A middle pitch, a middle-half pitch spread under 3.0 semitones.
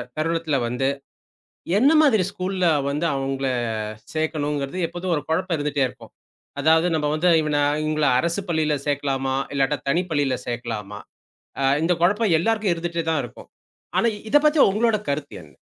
No: medium, 155 Hz; average, 4.4 semitones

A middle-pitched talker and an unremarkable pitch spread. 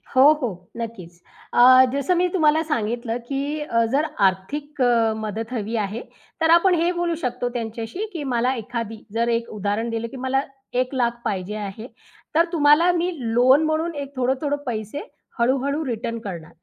No: high, 245 Hz; average, 4.6 semitones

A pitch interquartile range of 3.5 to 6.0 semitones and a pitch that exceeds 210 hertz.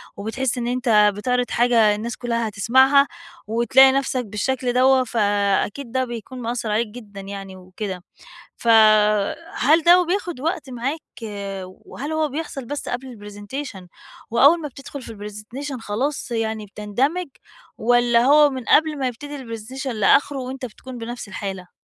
Yes: average, 4.0 semitones; high, 245 Hz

